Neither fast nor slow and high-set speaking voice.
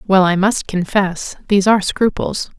Yes: average, 160 wpm; high, 195 Hz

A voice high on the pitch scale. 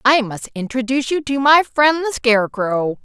Yes: very high, 255 Hz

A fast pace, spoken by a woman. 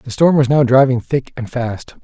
No: fast, 235 wpm; male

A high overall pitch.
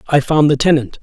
No: medium, 145 Hz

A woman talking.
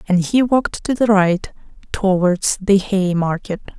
Yes: female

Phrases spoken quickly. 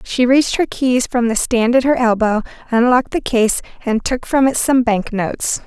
Yes: fast, 210 wpm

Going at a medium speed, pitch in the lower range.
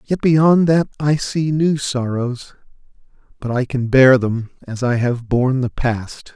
Yes: average, 170 wpm; low, 130 Hz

